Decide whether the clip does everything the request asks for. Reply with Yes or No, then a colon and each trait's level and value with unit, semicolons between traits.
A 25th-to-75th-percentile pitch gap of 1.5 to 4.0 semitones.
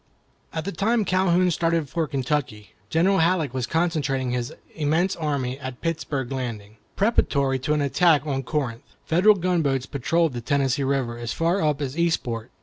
No: average, 4.4 semitones